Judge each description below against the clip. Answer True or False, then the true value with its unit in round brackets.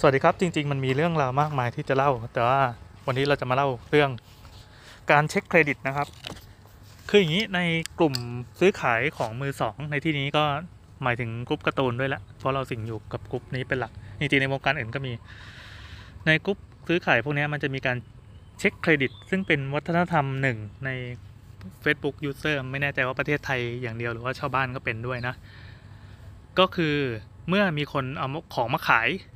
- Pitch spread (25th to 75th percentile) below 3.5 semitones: False (4.3 semitones)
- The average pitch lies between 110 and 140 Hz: True (135 Hz)